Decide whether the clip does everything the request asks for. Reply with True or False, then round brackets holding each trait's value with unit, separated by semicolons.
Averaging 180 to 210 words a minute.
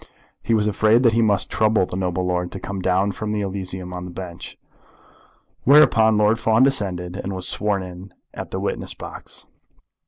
True (185 wpm)